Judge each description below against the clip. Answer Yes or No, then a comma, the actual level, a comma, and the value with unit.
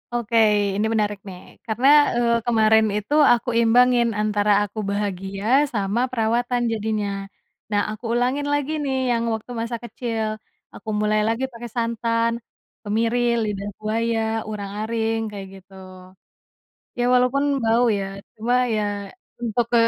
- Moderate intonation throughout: No, narrow, 2.2 semitones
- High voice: Yes, high, 225 Hz